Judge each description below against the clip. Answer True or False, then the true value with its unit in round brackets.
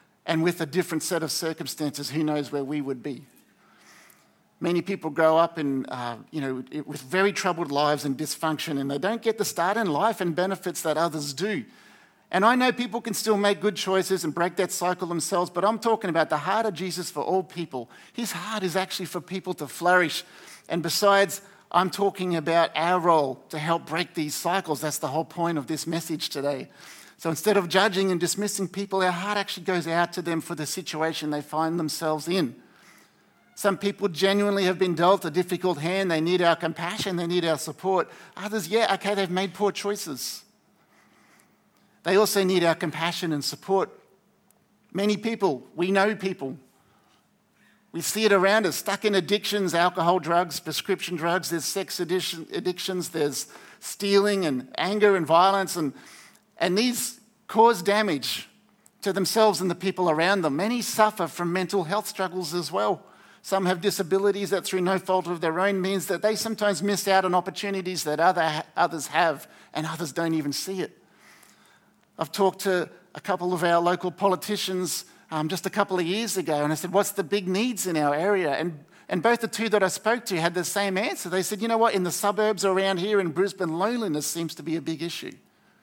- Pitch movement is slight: False (3.3 semitones)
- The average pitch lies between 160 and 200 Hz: True (185 Hz)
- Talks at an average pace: True (195 wpm)